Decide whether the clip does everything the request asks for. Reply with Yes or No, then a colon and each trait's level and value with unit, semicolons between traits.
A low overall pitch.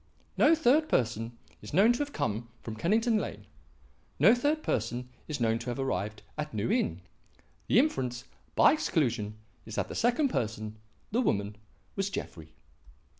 Yes: low, 125 Hz